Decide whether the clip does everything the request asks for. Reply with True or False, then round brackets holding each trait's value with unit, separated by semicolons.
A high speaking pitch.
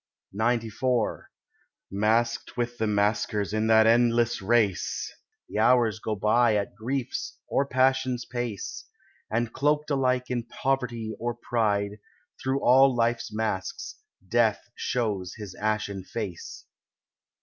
False (115 Hz)